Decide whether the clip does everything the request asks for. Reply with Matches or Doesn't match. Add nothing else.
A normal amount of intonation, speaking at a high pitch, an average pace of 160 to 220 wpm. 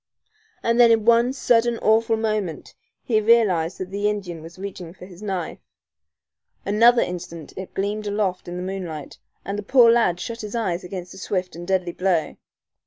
Matches